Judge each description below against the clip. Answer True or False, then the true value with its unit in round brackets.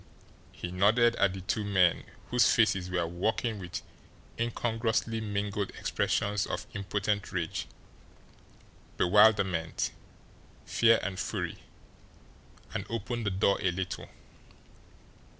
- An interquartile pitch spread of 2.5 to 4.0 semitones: True (3.2 semitones)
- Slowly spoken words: True (105 wpm)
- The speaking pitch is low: True (100 Hz)